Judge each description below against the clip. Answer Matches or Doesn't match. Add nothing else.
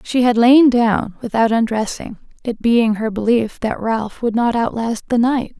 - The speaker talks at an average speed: Matches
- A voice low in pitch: Doesn't match